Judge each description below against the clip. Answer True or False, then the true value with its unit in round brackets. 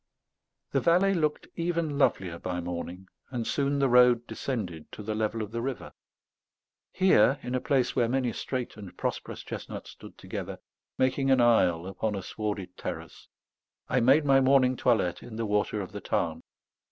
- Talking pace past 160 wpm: True (170 wpm)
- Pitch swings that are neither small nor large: True (4.6 semitones)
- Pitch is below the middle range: True (120 Hz)